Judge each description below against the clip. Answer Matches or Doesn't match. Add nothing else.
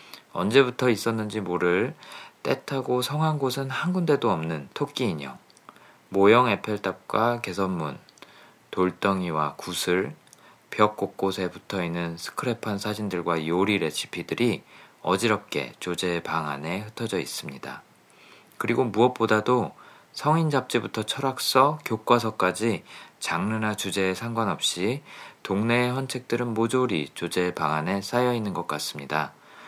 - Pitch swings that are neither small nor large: Matches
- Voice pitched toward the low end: Matches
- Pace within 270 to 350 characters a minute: Matches